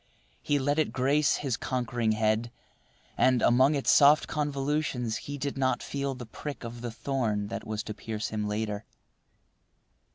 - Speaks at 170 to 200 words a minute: No, average, 160 wpm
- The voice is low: Yes, low, 125 Hz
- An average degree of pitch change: Yes, average, 4.2 semitones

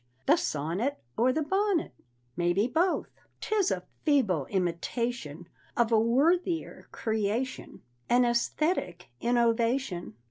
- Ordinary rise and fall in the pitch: No, wide, 7.3 semitones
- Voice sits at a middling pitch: No, high, 235 Hz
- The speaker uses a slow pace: Yes, slow, 105 wpm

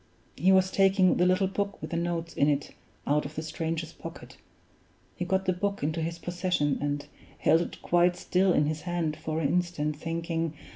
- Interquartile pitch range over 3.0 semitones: No, narrow, 2.6 semitones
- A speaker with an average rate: Yes, average, 195 wpm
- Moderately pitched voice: Yes, medium, 170 Hz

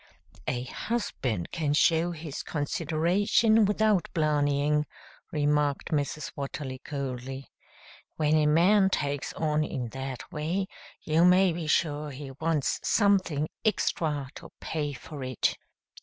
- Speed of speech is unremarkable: No, slow, 120 wpm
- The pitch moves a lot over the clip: No, average, 3.2 semitones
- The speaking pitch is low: No, medium, 150 Hz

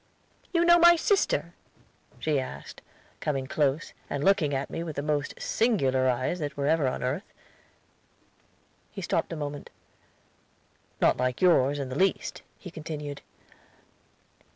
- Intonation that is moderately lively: Yes, average, 4.6 semitones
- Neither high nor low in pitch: Yes, medium, 150 Hz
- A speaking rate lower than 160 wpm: Yes, average, 140 wpm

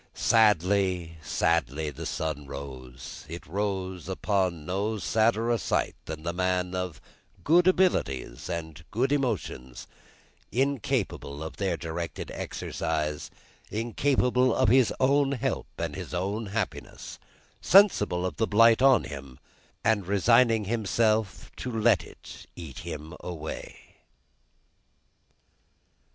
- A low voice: Yes, very low, 95 Hz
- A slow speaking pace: Yes, slow, 110 wpm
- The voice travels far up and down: Yes, wide, 6.1 semitones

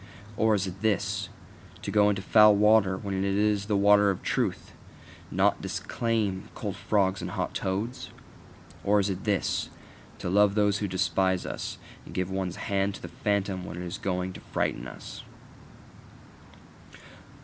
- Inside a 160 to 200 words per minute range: Yes, average, 165 wpm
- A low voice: Yes, low, 100 Hz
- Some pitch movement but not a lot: No, narrow, 1.7 semitones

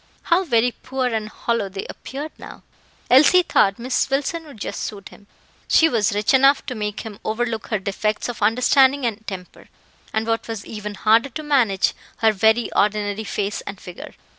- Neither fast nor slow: Yes, average, 180 wpm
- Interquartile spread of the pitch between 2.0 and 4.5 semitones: Yes, average, 3.9 semitones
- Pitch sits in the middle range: No, high, 225 Hz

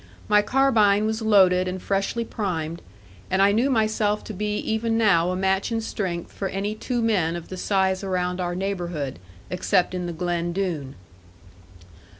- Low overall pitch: No, high, 195 Hz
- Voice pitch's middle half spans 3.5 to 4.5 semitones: No, average, 3.1 semitones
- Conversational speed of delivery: Yes, average, 165 wpm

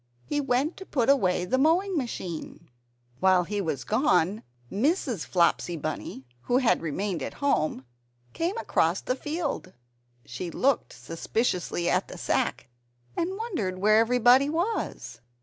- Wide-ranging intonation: Yes, wide, 8.4 semitones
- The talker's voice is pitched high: Yes, high, 225 Hz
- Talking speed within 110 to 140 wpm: Yes, slow, 135 wpm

